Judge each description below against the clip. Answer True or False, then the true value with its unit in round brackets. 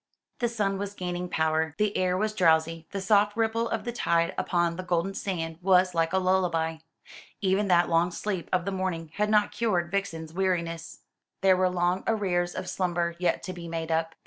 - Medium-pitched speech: True (180 Hz)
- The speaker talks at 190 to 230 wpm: True (195 wpm)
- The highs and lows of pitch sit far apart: False (2.7 semitones)